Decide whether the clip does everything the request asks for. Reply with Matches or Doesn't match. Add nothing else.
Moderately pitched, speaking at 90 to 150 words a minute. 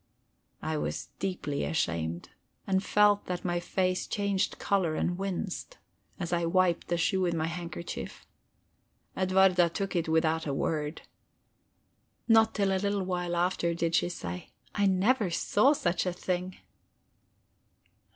Matches